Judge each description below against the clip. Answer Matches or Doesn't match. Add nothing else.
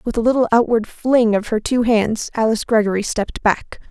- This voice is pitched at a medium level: Doesn't match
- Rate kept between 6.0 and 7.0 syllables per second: Doesn't match